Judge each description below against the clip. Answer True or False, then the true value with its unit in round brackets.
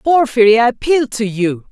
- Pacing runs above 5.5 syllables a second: False (5.0 syllables/s)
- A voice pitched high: True (240 Hz)